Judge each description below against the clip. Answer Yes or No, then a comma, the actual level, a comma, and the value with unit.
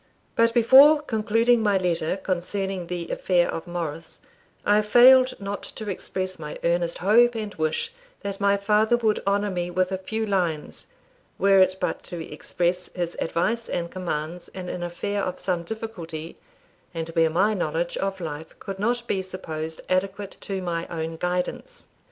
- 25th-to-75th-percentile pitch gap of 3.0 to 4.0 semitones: Yes, average, 3.6 semitones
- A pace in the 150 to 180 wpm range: Yes, average, 165 wpm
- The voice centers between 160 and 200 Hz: Yes, medium, 185 Hz